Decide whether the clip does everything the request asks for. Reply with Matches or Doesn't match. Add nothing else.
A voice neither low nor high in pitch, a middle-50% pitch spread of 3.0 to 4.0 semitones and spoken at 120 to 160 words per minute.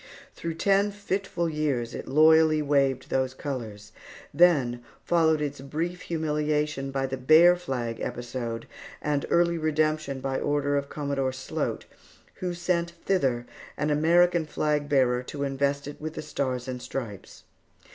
Matches